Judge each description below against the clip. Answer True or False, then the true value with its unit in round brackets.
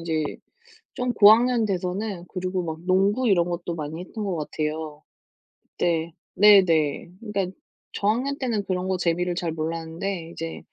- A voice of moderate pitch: True (180 Hz)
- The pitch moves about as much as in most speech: True (3.8 semitones)